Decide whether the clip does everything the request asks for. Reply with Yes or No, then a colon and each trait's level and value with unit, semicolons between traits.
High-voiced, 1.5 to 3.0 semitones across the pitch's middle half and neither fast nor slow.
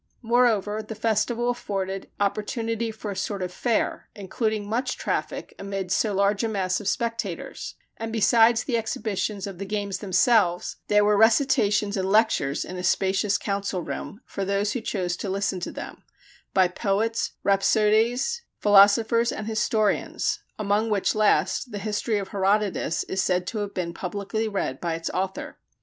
Yes: high, 205 Hz; narrow, 2.4 semitones; average, 160 wpm